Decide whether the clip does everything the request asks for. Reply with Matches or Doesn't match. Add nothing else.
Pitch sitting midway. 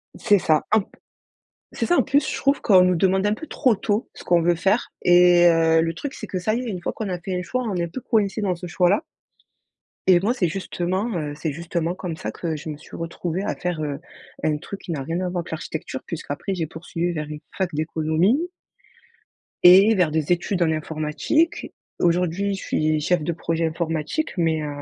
Matches